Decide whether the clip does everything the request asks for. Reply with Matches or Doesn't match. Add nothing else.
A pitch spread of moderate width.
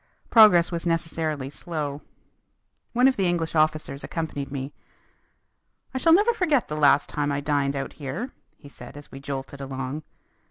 Matches